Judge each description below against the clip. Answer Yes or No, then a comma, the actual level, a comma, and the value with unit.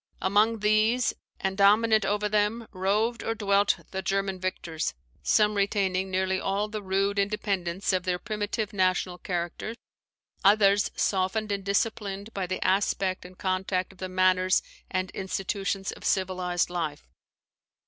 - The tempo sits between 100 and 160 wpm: Yes, average, 140 wpm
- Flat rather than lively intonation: Yes, narrow, 2.0 semitones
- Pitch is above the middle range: Yes, high, 195 Hz